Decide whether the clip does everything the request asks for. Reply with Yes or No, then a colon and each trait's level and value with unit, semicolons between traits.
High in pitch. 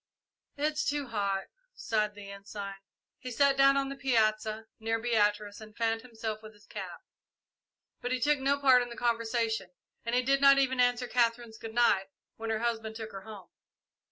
Yes: high, 230 Hz